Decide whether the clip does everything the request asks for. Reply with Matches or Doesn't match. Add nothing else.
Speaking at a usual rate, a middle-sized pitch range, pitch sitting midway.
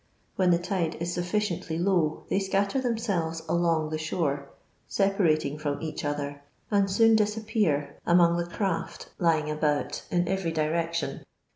Matches